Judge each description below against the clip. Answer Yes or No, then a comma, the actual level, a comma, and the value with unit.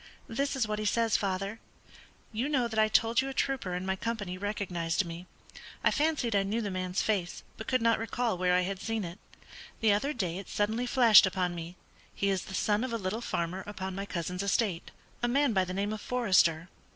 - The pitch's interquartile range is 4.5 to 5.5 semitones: No, average, 3.9 semitones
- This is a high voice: Yes, high, 205 Hz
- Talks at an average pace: No, fast, 220 wpm